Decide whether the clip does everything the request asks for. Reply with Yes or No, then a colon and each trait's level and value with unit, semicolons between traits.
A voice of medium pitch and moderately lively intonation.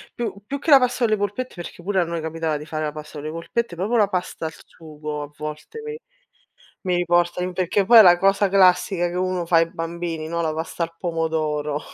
Yes: medium, 175 Hz; average, 3.3 semitones